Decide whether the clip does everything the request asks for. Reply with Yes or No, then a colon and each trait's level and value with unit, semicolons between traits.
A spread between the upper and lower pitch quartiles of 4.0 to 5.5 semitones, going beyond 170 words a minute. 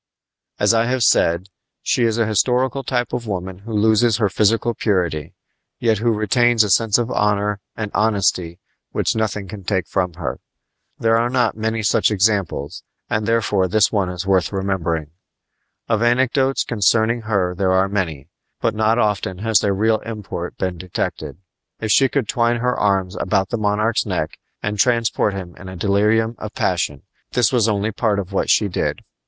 No: average, 3.2 semitones; average, 180 wpm